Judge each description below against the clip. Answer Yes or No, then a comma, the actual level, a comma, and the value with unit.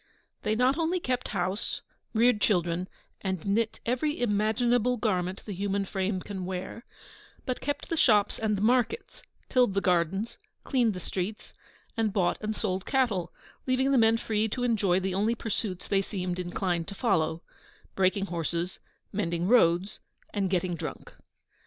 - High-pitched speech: Yes, high, 205 Hz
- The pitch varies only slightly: No, average, 4.0 semitones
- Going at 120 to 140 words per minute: No, average, 155 wpm